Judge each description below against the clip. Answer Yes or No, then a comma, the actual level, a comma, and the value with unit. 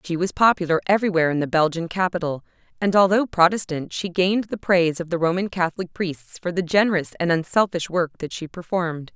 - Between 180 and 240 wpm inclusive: Yes, average, 190 wpm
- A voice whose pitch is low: No, medium, 175 Hz